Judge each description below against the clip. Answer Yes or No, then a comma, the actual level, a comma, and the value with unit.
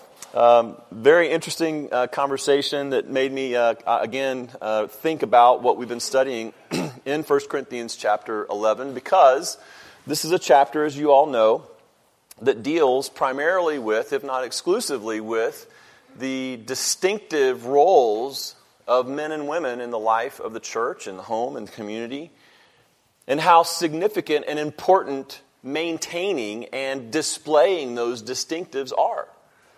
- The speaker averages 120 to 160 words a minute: Yes, average, 140 wpm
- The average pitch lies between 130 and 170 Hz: Yes, low, 135 Hz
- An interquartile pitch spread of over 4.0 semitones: Yes, average, 4.4 semitones